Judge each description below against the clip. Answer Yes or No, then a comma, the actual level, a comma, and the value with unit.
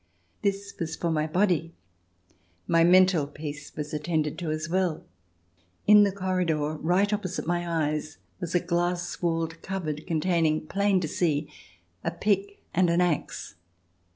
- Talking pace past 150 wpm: No, average, 145 wpm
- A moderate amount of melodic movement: Yes, average, 3.1 semitones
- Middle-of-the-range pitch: Yes, medium, 170 Hz